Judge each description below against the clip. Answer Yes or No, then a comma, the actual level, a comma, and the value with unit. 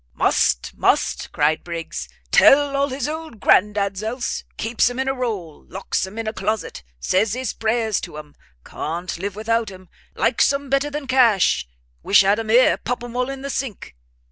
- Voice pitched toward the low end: No, high, 225 Hz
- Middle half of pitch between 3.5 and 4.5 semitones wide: No, average, 5.2 semitones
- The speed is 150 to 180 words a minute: No, average, 190 wpm